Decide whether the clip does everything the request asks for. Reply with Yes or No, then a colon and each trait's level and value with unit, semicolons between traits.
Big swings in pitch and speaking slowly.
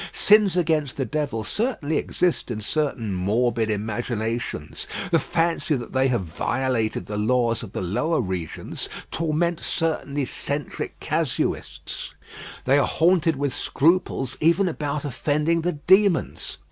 Yes: wide, 6.0 semitones; slow, 130 wpm